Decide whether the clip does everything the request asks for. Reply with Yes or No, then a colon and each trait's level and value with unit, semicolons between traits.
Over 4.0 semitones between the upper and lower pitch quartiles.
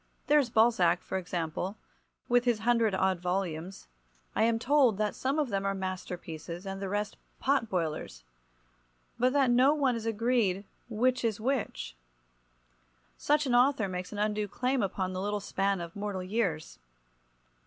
Yes: average, 4.6 semitones